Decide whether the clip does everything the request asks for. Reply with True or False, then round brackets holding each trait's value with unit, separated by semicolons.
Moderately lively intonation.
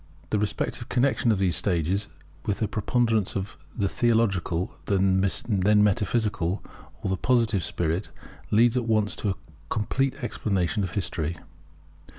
True (3.2 semitones)